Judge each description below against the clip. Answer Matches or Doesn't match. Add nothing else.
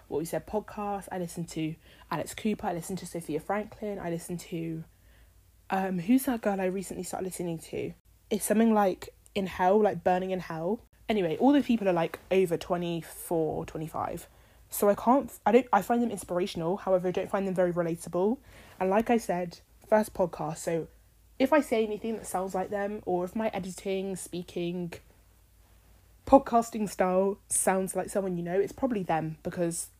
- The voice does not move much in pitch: Doesn't match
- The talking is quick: Doesn't match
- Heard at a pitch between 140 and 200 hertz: Matches